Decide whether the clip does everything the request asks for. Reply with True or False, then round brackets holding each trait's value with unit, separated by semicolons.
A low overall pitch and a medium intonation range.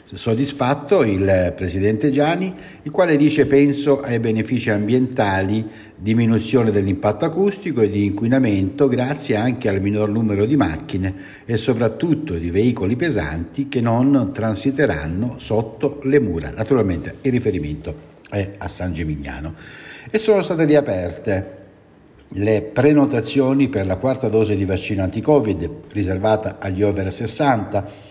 False (110 Hz; 5.9 semitones)